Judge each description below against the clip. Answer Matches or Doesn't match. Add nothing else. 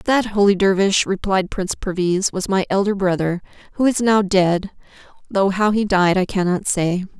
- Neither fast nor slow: Matches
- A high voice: Matches